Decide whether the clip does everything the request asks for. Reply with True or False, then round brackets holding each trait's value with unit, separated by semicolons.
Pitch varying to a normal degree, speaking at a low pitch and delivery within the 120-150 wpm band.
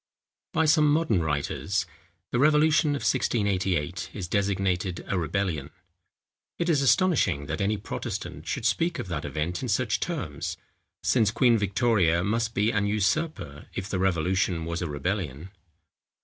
False (6.0 semitones; 100 Hz; 145 wpm)